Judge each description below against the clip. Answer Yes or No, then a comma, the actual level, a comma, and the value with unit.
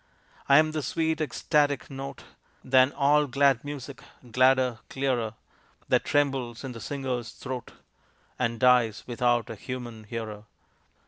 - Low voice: Yes, low, 130 Hz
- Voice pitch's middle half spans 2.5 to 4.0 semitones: Yes, average, 2.9 semitones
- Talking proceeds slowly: Yes, slow, 130 wpm